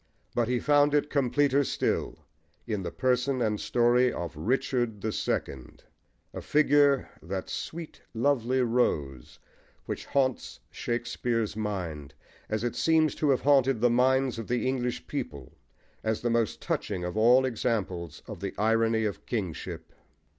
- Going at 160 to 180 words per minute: No, average, 145 wpm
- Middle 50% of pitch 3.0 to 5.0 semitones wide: Yes, average, 3.8 semitones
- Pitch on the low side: Yes, low, 120 Hz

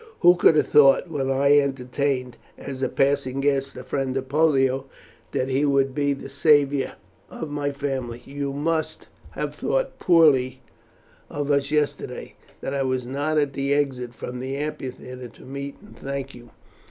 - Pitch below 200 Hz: Yes, medium, 140 Hz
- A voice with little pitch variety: Yes, narrow, 1.7 semitones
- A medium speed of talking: Yes, average, 165 wpm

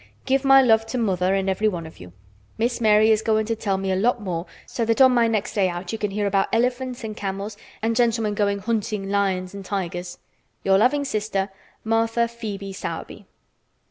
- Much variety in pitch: No, average, 2.9 semitones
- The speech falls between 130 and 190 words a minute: No, average, 200 wpm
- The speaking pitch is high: Yes, high, 210 Hz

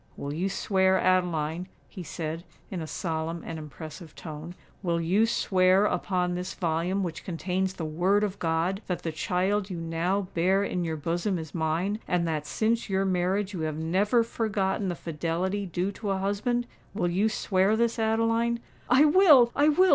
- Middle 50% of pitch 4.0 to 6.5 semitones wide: No, average, 3.6 semitones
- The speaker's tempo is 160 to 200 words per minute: Yes, average, 170 wpm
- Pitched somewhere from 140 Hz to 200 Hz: Yes, medium, 185 Hz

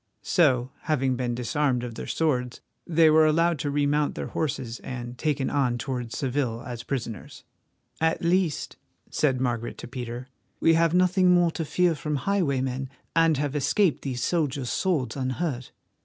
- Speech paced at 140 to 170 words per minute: Yes, average, 155 wpm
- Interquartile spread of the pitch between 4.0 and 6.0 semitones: Yes, average, 4.5 semitones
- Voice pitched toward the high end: No, medium, 140 Hz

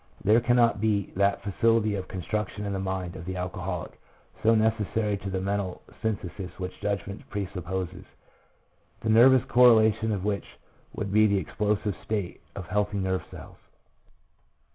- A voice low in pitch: Yes, low, 100 Hz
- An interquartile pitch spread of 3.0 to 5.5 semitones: No, narrow, 2.5 semitones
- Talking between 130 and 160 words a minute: Yes, average, 145 wpm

